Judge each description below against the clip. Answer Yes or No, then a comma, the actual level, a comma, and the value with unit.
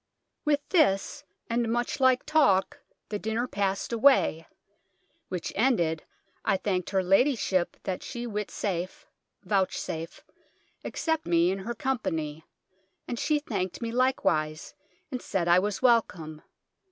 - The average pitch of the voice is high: Yes, high, 205 Hz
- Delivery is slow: Yes, slow, 130 wpm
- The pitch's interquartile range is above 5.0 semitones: Yes, wide, 5.5 semitones